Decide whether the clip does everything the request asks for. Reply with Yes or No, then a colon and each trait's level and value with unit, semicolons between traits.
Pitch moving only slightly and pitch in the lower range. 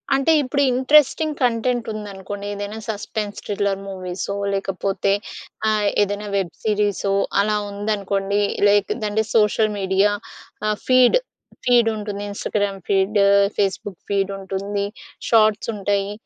No: narrow, 1.7 semitones; high, 205 Hz